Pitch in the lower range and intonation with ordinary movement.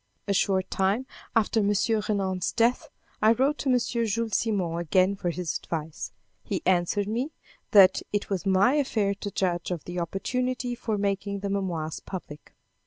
No: high, 200 Hz; average, 3.7 semitones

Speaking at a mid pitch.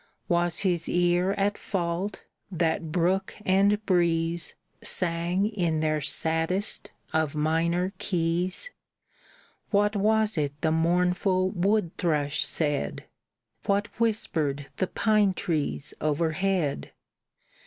Yes: medium, 175 Hz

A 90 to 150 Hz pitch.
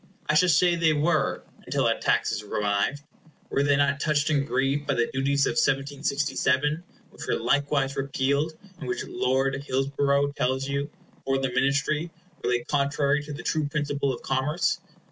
Yes: medium, 140 Hz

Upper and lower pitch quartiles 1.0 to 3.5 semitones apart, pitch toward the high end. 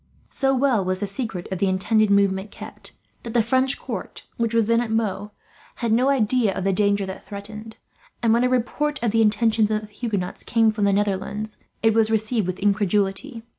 Yes: narrow, 2.5 semitones; high, 215 Hz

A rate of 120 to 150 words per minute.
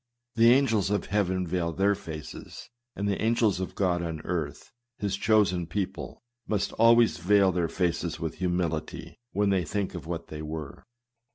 No: average, 165 wpm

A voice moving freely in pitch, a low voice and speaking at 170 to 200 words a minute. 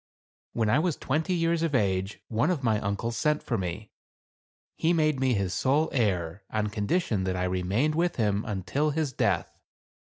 Yes: wide, 7.3 semitones; low, 115 Hz; average, 175 wpm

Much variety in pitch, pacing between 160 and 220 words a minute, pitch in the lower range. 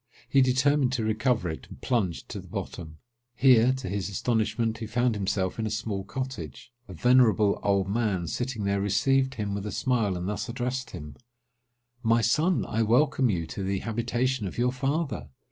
No: average, 4.0 semitones; average, 180 wpm; low, 115 Hz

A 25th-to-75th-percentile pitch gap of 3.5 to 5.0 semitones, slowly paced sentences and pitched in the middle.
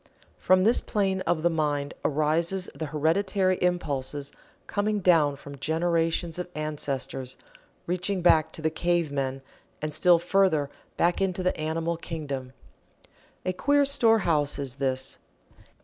Yes: average, 4.1 semitones; slow, 130 wpm; medium, 165 Hz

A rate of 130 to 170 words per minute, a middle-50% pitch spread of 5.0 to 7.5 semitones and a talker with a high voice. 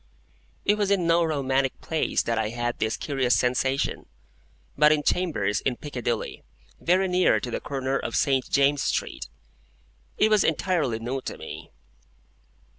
No: average, 150 wpm; wide, 5.4 semitones; low, 135 Hz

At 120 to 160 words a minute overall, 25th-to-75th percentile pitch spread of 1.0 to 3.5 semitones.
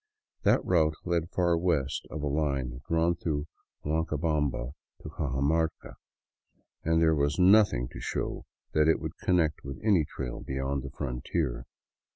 Yes: average, 145 wpm; average, 3.2 semitones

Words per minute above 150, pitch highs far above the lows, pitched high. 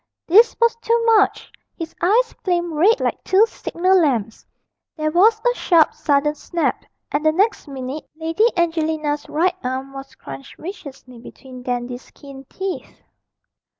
No: average, 145 wpm; wide, 5.7 semitones; very high, 320 Hz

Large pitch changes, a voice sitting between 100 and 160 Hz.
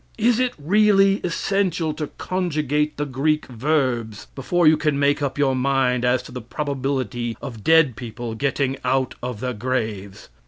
No: average, 3.8 semitones; medium, 140 Hz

